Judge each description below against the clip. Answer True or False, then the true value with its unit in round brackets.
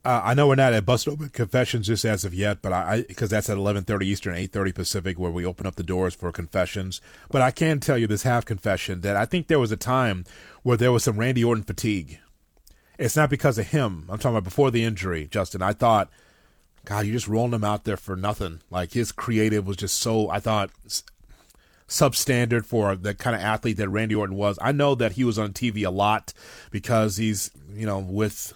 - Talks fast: True (230 wpm)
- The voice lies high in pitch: False (110 Hz)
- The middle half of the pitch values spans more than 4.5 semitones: False (3.4 semitones)